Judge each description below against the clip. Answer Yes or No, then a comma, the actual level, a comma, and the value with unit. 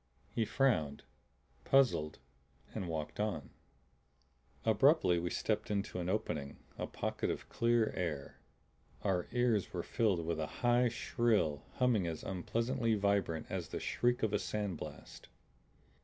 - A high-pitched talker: No, low, 100 Hz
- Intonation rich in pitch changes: Yes, wide, 5.8 semitones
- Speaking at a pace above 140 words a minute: No, slow, 135 wpm